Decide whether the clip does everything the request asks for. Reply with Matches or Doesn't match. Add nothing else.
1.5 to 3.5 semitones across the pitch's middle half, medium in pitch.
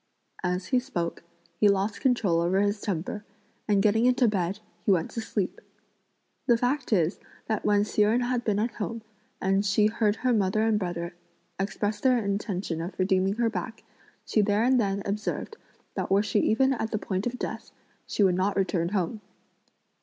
Doesn't match